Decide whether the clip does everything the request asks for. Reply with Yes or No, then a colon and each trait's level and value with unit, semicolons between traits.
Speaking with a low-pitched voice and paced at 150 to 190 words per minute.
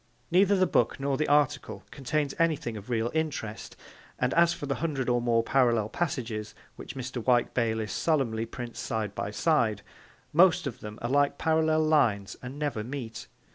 Yes: low, 130 Hz; average, 175 wpm